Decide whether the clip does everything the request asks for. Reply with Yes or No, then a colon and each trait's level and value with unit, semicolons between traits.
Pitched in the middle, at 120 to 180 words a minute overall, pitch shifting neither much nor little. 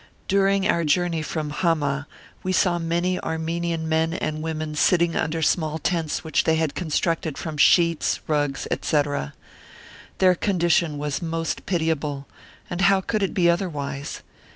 No: medium, 165 Hz; average, 145 wpm; narrow, 2.3 semitones